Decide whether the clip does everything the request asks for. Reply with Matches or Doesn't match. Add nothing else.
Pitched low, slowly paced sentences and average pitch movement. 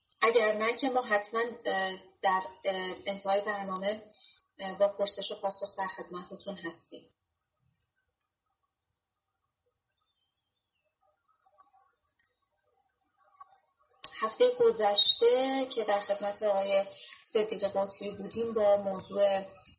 Doesn't match